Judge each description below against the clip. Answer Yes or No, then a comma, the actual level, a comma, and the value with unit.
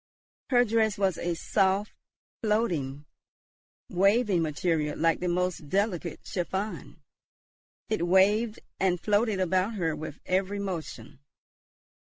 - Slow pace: Yes, slow, 110 wpm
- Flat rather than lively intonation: No, average, 3.7 semitones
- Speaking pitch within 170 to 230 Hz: Yes, high, 190 Hz